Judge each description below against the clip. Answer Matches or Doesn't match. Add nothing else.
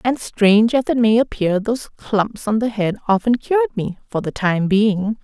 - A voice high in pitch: Matches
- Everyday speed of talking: Matches